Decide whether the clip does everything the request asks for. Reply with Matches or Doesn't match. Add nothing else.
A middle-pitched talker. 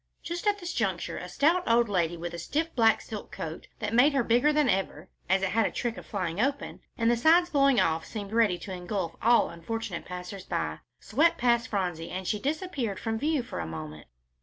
Doesn't match